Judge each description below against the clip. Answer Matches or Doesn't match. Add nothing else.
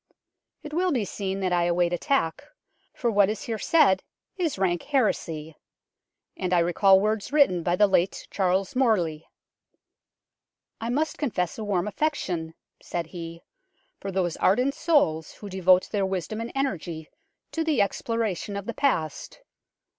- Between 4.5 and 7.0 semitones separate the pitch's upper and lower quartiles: Matches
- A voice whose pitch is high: Matches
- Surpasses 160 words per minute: Doesn't match